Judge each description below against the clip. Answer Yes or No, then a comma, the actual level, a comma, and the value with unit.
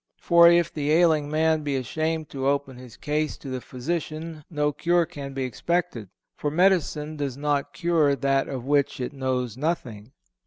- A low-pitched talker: No, medium, 150 Hz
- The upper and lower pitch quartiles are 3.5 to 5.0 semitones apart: No, average, 3.1 semitones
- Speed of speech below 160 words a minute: No, average, 170 wpm